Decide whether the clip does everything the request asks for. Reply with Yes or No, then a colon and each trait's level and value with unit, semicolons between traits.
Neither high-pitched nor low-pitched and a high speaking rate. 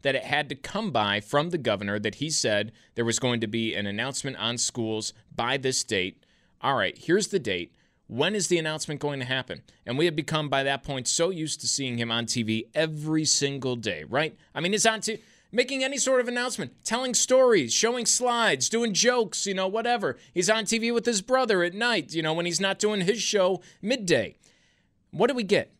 Yes: medium, 155 Hz; fast, 220 wpm